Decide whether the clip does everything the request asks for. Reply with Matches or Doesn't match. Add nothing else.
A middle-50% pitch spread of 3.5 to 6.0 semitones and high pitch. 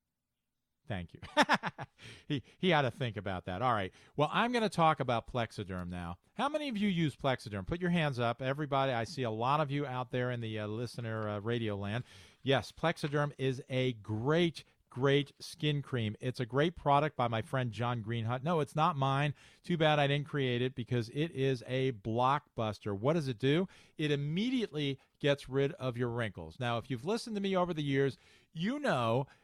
Doesn't match